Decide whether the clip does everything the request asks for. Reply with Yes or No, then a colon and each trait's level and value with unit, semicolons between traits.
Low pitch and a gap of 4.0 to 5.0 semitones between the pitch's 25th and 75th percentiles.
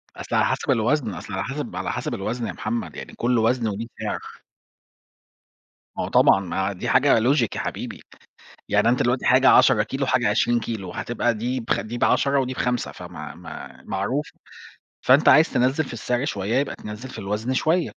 No: low, 120 Hz; average, 3.3 semitones